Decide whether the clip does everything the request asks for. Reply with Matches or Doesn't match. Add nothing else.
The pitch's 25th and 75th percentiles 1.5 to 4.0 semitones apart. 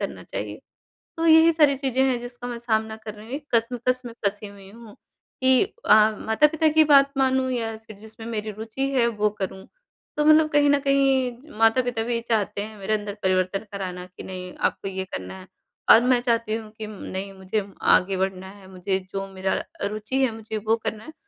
Doesn't match